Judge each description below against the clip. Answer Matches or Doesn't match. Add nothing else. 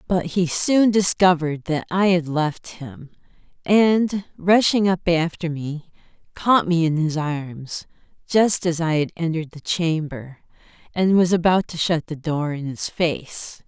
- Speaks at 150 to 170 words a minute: Matches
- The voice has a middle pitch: Matches